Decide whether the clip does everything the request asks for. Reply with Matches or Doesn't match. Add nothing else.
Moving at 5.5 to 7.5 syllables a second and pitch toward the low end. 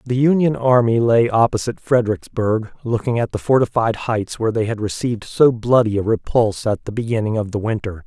Matches